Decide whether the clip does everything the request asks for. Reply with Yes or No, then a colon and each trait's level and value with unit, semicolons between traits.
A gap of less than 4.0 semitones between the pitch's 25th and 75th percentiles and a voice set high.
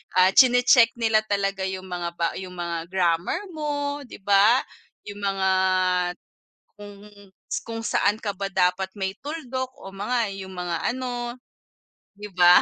No: average, 4.4 semitones; high, 200 Hz